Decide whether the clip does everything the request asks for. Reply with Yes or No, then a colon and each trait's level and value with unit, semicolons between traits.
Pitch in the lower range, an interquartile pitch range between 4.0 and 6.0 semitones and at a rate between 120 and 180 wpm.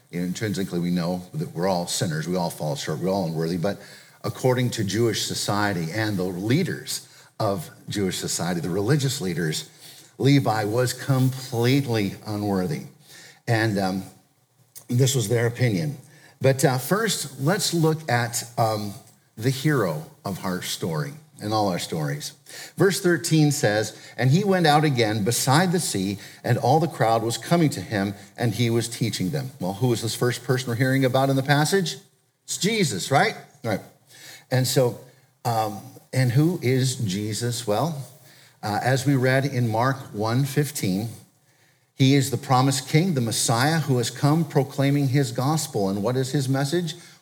Yes: low, 130 Hz; average, 4.7 semitones; average, 165 wpm